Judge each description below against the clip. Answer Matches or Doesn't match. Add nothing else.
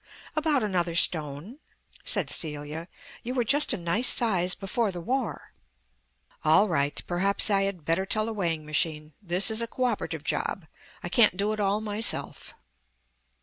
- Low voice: Doesn't match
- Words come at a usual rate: Matches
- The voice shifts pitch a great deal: Doesn't match